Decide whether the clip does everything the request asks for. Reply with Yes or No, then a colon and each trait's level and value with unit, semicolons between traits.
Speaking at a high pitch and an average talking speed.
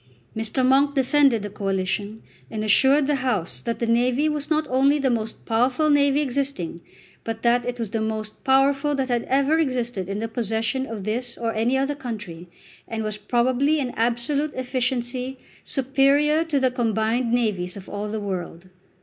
Yes: high, 245 Hz; average, 175 wpm